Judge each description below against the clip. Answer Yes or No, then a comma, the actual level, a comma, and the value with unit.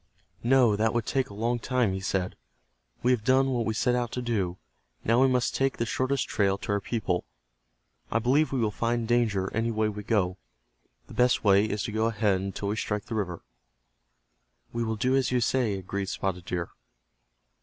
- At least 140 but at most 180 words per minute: No, average, 200 wpm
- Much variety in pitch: No, average, 3.5 semitones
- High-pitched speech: No, low, 110 Hz